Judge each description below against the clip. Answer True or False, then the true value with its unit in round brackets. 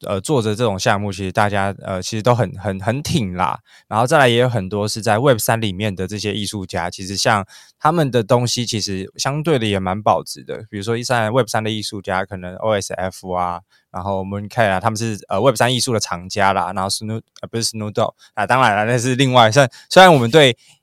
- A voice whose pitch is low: True (110 Hz)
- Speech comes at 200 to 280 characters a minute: False (375 characters per minute)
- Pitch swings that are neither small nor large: True (3.9 semitones)